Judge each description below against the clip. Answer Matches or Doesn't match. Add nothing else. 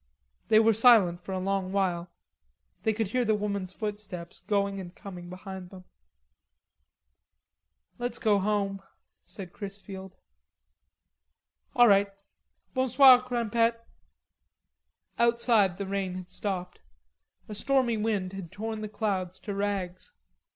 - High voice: Matches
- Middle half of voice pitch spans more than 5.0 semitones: Doesn't match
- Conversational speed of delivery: Doesn't match